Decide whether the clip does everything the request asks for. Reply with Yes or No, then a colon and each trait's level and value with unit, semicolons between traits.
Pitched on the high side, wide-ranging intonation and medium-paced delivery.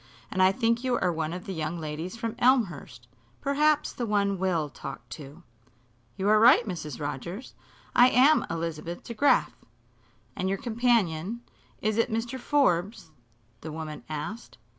Yes: high, 195 Hz; wide, 6.4 semitones; average, 150 wpm